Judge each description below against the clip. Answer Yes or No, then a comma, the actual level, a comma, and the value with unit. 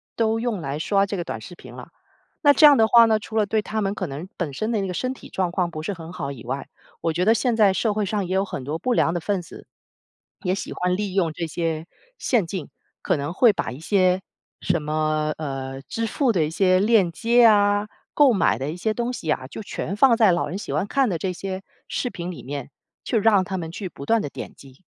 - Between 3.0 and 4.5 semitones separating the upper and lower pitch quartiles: No, average, 5.1 semitones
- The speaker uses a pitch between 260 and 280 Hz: No, high, 190 Hz